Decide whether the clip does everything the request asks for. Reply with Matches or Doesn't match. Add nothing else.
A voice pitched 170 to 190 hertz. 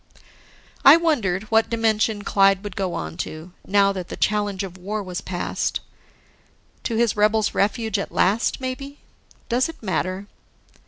Doesn't match